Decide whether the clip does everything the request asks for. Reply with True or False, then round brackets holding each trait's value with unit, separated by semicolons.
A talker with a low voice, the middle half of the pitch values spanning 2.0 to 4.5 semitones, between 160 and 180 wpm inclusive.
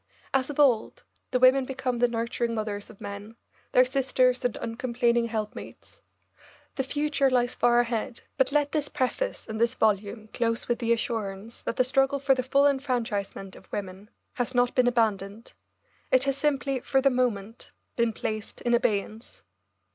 False (240 Hz; 3.0 semitones; 165 wpm)